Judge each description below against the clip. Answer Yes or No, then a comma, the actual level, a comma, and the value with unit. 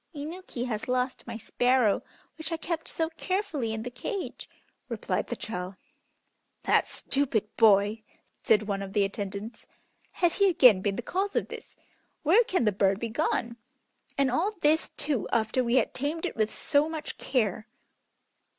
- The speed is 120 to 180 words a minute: Yes, average, 165 wpm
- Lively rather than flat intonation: Yes, wide, 6.7 semitones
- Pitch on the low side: No, high, 245 Hz